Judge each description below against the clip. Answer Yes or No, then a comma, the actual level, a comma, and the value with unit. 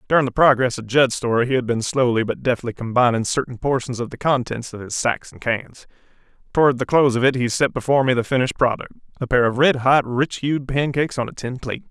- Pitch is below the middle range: Yes, low, 125 Hz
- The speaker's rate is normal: No, fast, 230 wpm